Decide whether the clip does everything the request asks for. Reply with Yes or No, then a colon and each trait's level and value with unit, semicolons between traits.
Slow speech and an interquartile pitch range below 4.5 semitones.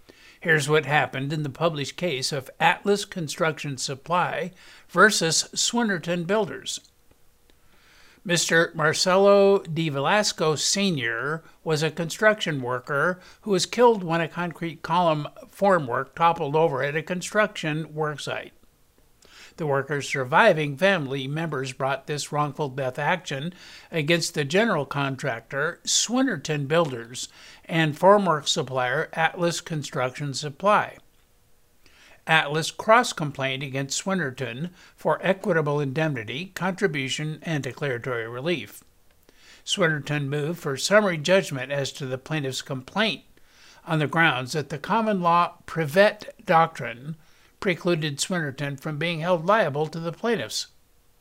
Yes: slow, 115 wpm; average, 4.1 semitones